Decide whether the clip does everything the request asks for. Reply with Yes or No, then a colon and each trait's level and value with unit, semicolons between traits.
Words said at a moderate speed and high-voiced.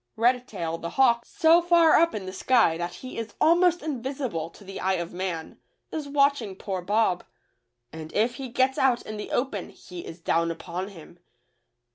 Yes: average, 185 wpm; high, 220 Hz